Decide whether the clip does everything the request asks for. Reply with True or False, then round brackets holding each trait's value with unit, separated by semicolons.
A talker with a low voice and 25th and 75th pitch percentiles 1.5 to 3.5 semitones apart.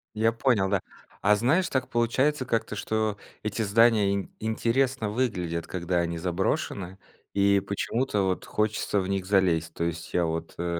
False (100 Hz; 4.0 semitones)